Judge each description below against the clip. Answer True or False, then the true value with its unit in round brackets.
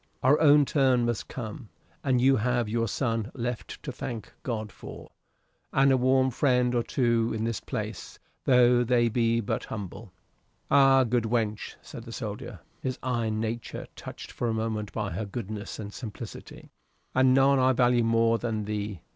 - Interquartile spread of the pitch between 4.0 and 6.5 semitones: False (2.6 semitones)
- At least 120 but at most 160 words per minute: False (170 wpm)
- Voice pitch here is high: False (120 Hz)